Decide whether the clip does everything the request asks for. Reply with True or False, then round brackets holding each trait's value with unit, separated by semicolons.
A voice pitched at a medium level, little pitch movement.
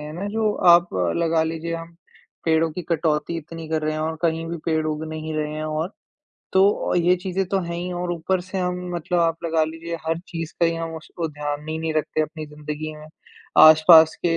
True (165 Hz; 1.6 semitones)